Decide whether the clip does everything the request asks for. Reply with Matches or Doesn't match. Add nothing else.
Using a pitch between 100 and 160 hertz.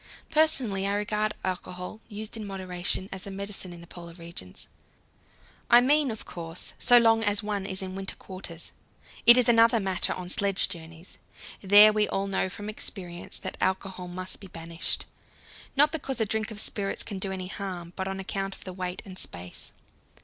Doesn't match